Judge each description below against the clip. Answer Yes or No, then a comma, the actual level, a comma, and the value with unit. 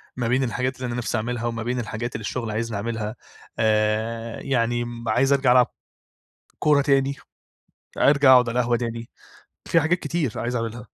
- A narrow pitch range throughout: Yes, narrow, 2.2 semitones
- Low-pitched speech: Yes, low, 120 Hz